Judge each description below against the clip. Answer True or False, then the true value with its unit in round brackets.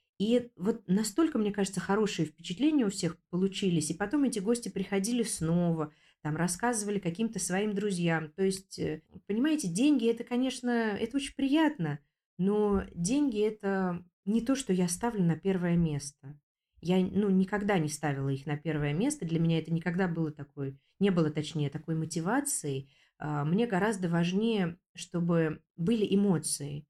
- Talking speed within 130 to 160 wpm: True (150 wpm)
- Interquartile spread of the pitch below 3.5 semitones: False (4.8 semitones)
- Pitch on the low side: False (185 Hz)